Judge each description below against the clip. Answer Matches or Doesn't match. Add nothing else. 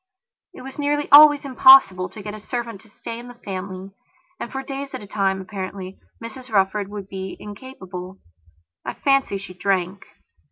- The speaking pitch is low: Doesn't match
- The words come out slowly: Doesn't match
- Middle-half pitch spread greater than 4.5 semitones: Matches